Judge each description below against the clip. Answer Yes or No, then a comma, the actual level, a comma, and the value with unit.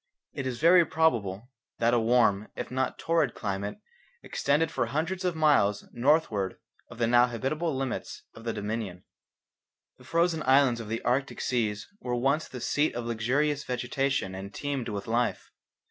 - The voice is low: Yes, low, 125 Hz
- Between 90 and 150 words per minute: No, average, 165 wpm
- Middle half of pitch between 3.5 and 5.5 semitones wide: Yes, average, 4.5 semitones